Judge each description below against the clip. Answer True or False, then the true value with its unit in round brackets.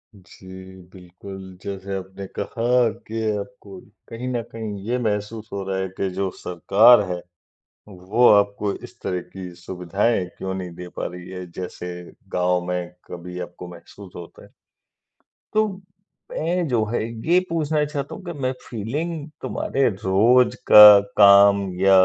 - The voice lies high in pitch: False (100 Hz)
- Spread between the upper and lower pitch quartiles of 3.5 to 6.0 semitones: True (4.1 semitones)